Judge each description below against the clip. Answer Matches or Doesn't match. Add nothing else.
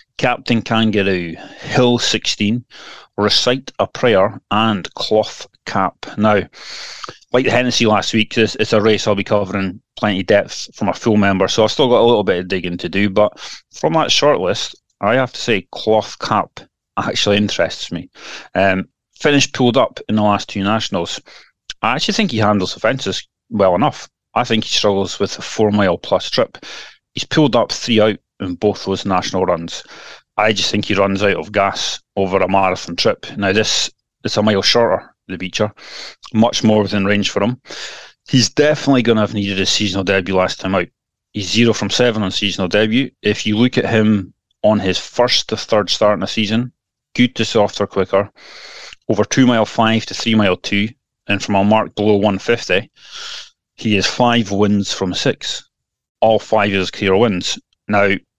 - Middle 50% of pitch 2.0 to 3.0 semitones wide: Matches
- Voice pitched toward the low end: Matches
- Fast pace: Doesn't match